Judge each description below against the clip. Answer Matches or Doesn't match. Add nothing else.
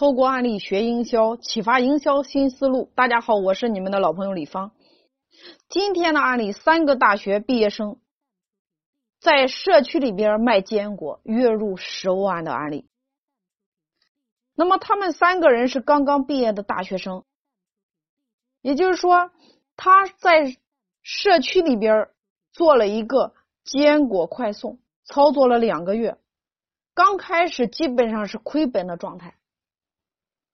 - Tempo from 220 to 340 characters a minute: Doesn't match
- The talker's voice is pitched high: Matches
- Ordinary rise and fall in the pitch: Doesn't match